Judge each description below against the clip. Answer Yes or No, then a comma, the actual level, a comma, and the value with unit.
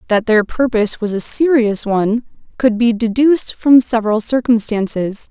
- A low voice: No, high, 230 Hz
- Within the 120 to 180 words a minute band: Yes, average, 145 wpm